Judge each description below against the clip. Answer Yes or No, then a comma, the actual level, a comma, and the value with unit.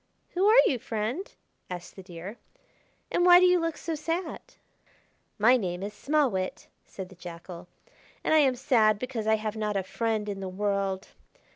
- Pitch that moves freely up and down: Yes, wide, 7.3 semitones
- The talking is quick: No, average, 180 wpm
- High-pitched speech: Yes, high, 215 Hz